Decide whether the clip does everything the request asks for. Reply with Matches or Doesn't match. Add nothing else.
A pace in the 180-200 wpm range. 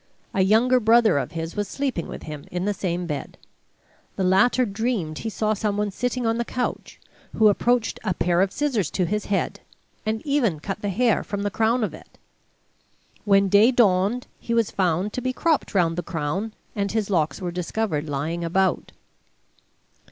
Matches